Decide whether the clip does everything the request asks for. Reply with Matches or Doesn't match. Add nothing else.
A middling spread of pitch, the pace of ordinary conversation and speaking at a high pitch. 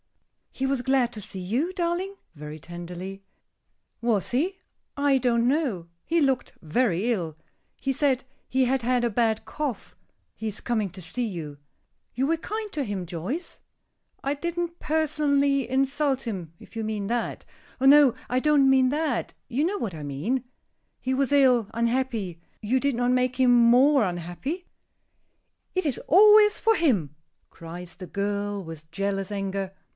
Doesn't match